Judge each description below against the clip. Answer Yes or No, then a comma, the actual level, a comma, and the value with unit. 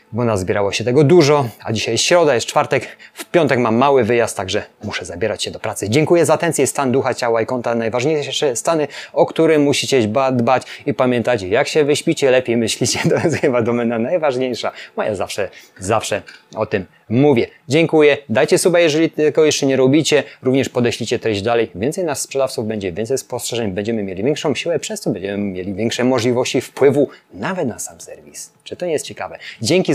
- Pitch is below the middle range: Yes, low, 130 Hz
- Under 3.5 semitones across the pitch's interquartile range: No, average, 4.3 semitones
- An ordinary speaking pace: No, fast, 190 wpm